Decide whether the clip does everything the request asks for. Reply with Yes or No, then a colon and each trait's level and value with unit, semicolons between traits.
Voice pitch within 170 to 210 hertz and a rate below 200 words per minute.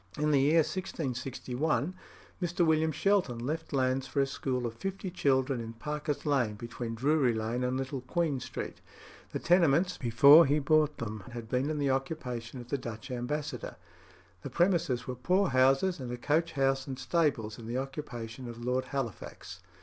No: low, 135 Hz; average, 175 wpm